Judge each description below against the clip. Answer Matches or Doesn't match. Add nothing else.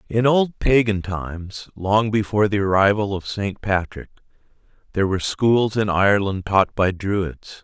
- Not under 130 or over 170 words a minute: Matches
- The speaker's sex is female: Doesn't match